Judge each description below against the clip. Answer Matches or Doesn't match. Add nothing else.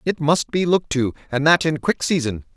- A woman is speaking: Doesn't match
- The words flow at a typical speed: Doesn't match